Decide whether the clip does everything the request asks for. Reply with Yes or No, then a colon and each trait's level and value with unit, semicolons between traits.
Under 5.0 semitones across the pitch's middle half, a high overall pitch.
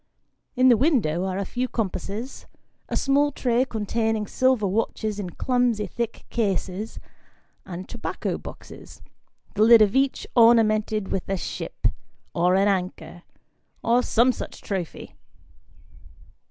Yes: average, 4.0 semitones; high, 220 Hz